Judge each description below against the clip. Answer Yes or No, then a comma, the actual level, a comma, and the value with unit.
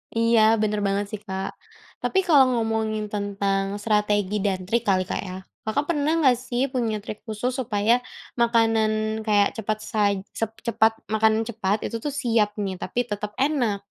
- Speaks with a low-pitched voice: No, high, 215 Hz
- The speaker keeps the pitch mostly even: Yes, narrow, 2.1 semitones